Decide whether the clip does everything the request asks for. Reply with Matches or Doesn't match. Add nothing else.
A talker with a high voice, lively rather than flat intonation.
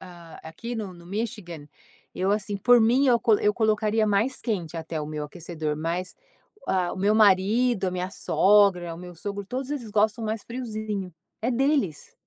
Doesn't match